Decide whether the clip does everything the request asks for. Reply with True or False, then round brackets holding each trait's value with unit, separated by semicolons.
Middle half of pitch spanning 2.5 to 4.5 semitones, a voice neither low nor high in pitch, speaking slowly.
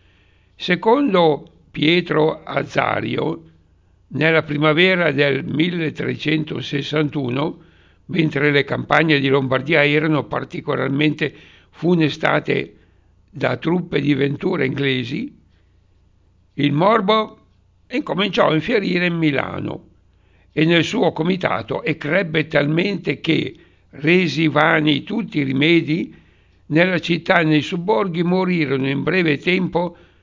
True (4.1 semitones; 150 Hz; 95 wpm)